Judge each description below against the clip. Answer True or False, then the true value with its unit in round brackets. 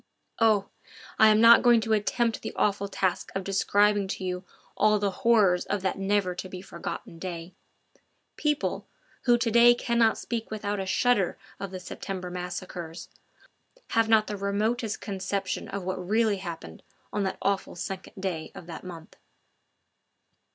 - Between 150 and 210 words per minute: True (160 wpm)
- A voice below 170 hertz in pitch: False (200 Hz)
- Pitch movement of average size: True (3.0 semitones)